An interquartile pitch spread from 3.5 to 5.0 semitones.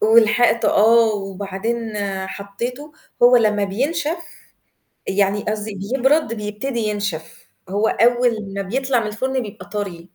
No: average, 3.1 semitones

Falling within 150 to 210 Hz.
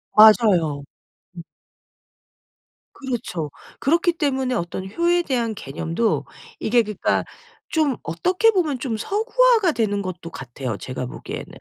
No: high, 230 Hz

